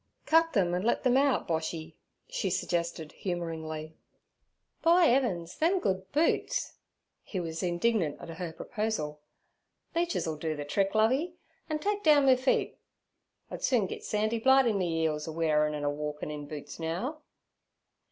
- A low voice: No, medium, 180 Hz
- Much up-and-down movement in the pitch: Yes, wide, 8.3 semitones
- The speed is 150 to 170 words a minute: Yes, average, 160 wpm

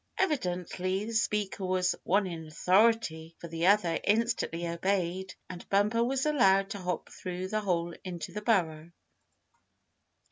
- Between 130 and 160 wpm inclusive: Yes, average, 140 wpm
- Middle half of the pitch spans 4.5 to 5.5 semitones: No, average, 3.4 semitones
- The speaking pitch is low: No, medium, 185 Hz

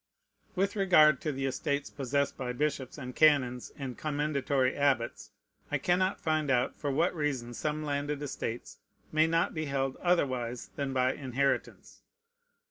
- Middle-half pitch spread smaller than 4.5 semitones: Yes, average, 2.8 semitones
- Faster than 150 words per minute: No, average, 145 wpm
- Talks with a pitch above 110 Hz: Yes, medium, 140 Hz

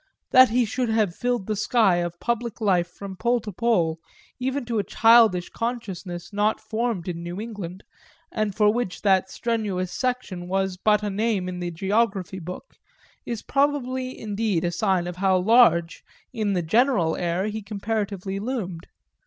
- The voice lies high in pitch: Yes, high, 205 Hz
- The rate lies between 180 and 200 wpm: No, average, 165 wpm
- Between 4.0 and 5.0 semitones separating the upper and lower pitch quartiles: Yes, average, 4.3 semitones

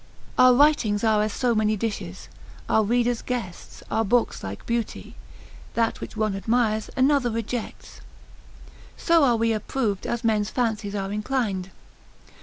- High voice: Yes, high, 225 Hz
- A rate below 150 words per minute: Yes, average, 140 wpm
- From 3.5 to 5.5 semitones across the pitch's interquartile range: No, average, 2.8 semitones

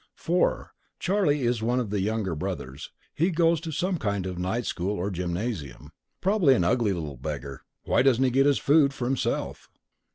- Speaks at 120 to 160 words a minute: No, average, 185 wpm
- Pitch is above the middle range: No, low, 115 Hz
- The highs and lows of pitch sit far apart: Yes, wide, 7.9 semitones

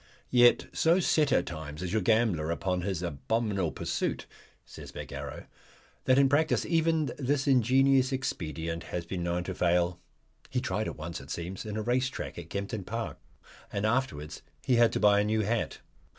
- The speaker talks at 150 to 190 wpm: Yes, average, 180 wpm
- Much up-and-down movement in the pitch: Yes, wide, 6.7 semitones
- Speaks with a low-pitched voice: Yes, low, 105 Hz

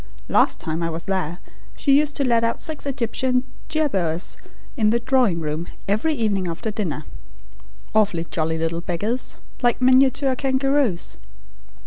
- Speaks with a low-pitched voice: No, high, 220 Hz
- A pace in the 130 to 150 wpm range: Yes, average, 140 wpm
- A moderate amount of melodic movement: No, wide, 7.5 semitones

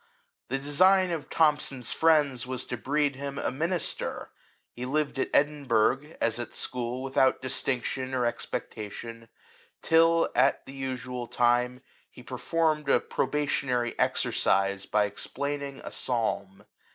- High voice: No, low, 130 Hz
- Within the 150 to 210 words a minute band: No, average, 140 wpm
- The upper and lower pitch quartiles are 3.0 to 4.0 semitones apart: Yes, average, 3.3 semitones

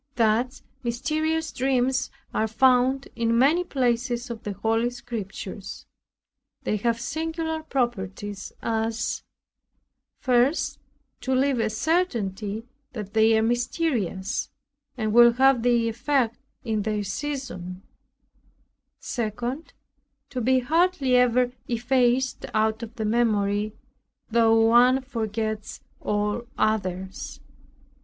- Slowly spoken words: Yes, slow, 105 wpm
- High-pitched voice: Yes, high, 235 Hz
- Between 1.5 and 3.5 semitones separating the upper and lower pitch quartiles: Yes, average, 3.2 semitones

